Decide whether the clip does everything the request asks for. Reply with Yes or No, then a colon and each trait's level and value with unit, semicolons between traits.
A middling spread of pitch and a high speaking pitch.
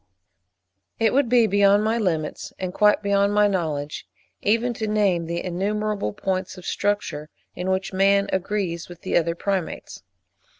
Yes: average, 3.0 semitones; high, 195 Hz